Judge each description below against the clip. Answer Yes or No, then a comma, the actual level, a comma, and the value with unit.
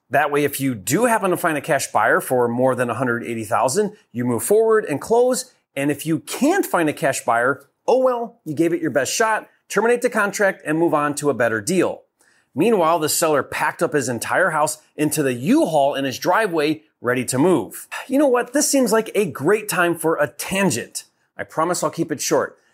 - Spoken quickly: Yes, fast, 215 wpm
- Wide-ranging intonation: Yes, wide, 7.5 semitones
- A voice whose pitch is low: No, medium, 160 Hz